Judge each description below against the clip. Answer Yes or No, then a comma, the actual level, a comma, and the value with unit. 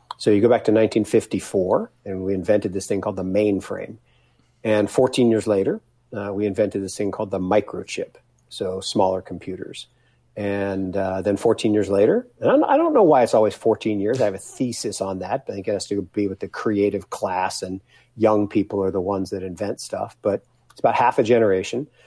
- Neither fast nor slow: No, fast, 210 wpm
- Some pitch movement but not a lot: No, narrow, 1.9 semitones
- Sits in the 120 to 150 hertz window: No, low, 100 Hz